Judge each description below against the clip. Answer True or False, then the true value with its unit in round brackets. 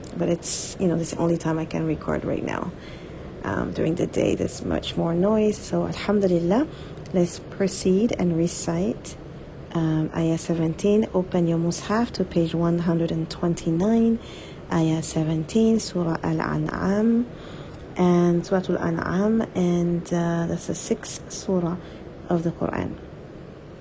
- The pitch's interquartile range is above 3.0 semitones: False (2.5 semitones)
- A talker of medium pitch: True (175 Hz)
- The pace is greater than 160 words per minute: False (135 wpm)